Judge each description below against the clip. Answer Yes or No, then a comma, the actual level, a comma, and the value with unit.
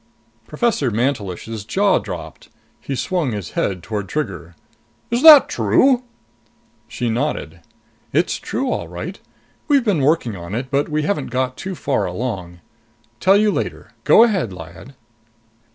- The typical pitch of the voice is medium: No, low, 130 Hz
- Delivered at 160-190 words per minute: No, average, 140 wpm